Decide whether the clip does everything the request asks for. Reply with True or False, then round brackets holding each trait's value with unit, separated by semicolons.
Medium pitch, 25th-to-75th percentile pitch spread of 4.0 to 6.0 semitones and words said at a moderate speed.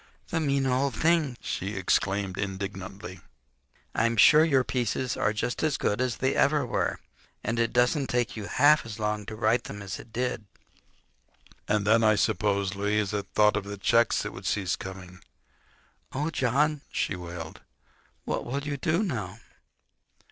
False (110 Hz; 4.8 semitones; 160 wpm)